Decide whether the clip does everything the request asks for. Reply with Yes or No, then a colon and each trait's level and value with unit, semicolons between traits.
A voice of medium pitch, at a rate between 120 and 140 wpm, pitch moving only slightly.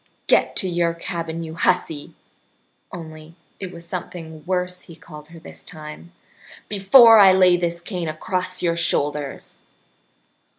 Yes: medium, 170 Hz; slow, 135 wpm; narrow, 2.3 semitones